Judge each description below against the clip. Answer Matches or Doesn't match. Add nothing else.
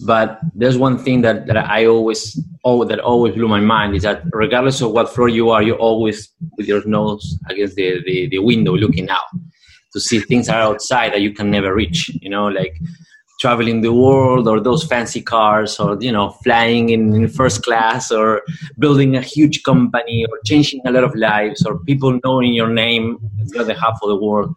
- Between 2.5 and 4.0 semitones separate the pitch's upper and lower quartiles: Matches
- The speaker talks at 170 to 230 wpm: Matches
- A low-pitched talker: Matches